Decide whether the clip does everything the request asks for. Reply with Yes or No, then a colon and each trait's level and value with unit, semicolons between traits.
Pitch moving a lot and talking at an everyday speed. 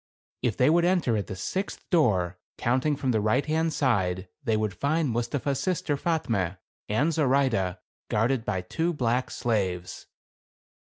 Yes: wide, 6.7 semitones; average, 150 wpm